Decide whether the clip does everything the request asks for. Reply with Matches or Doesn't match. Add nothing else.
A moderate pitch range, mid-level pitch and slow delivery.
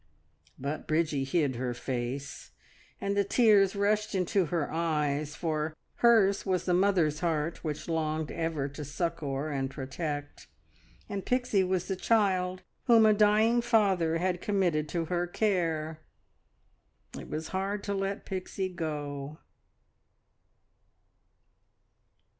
Matches